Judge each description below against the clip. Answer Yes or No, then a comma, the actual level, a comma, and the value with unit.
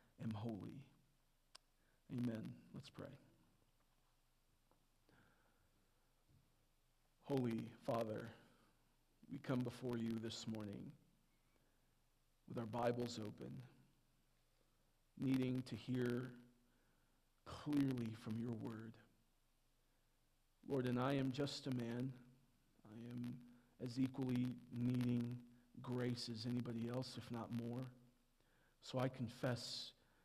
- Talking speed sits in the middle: No, slow, 90 wpm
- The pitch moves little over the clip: Yes, narrow, 1.7 semitones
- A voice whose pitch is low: Yes, low, 120 Hz